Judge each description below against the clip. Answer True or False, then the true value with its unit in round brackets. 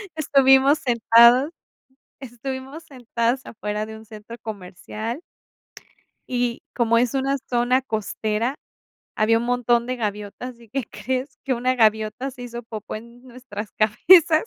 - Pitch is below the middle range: False (240 Hz)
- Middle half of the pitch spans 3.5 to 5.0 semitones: False (3.0 semitones)